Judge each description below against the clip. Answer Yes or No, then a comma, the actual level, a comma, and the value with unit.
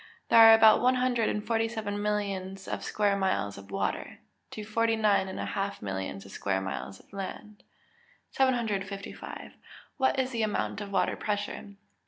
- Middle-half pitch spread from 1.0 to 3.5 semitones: Yes, narrow, 2.6 semitones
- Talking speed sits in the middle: Yes, average, 175 wpm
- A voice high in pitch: Yes, high, 205 Hz